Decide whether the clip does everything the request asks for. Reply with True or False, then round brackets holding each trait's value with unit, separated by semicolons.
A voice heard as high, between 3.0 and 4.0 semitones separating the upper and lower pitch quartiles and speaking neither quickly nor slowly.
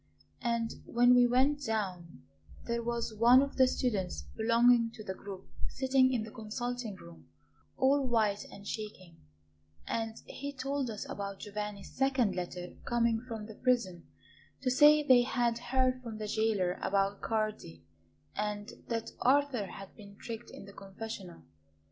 True (225 Hz; 3.6 semitones; 155 wpm)